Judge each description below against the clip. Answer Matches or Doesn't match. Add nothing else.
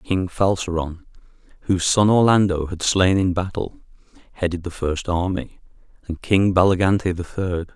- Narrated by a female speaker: Doesn't match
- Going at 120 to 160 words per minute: Matches